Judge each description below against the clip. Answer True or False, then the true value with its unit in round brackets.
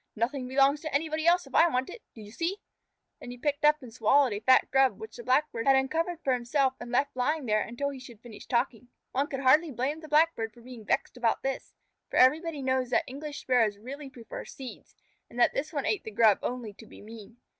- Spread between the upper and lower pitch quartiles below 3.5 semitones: False (3.8 semitones)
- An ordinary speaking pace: False (230 wpm)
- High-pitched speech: True (260 Hz)